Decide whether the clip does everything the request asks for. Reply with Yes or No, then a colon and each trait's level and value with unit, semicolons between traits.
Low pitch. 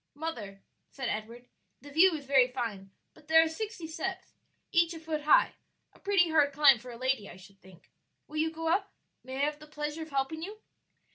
No: very high, 295 Hz